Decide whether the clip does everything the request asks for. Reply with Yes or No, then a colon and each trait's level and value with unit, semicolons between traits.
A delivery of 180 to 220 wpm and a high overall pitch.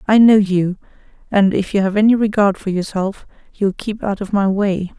Yes: fast, 205 wpm; high, 200 Hz